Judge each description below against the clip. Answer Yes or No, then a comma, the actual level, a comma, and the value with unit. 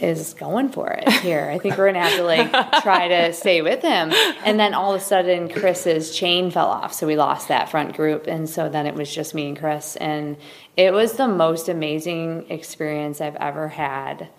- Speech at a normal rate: No, fast, 215 wpm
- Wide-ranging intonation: No, average, 3.9 semitones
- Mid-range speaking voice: Yes, medium, 165 Hz